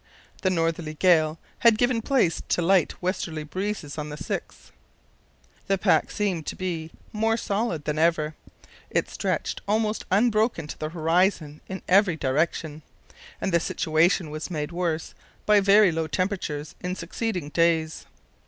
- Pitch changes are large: No, average, 4.0 semitones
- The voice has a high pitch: No, medium, 170 Hz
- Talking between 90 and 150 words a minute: Yes, average, 145 wpm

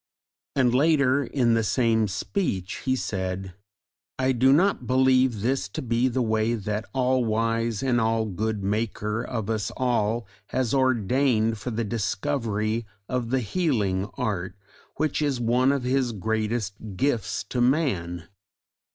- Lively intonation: No, average, 3.4 semitones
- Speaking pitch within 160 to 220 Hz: No, low, 115 Hz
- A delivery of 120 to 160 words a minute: Yes, average, 145 wpm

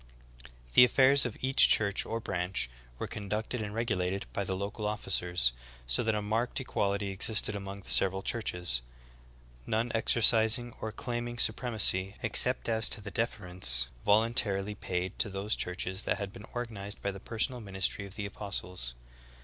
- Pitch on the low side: Yes, low, 105 Hz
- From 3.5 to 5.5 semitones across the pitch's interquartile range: No, average, 2.9 semitones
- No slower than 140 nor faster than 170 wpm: Yes, average, 165 wpm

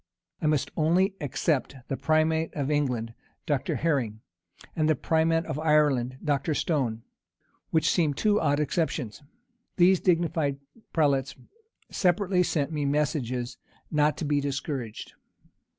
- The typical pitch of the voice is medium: Yes, medium, 150 Hz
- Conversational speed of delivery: No, slow, 125 wpm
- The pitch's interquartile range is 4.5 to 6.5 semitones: No, average, 2.8 semitones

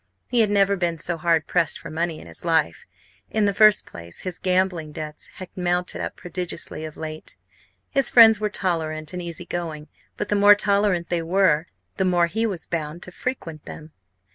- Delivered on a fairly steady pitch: No, average, 3.8 semitones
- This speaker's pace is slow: No, average, 190 wpm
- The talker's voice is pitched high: No, medium, 175 Hz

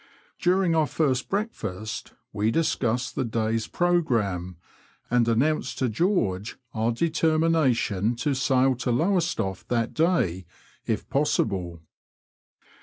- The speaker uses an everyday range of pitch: No, wide, 6.7 semitones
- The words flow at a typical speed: No, slow, 110 wpm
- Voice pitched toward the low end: Yes, low, 125 Hz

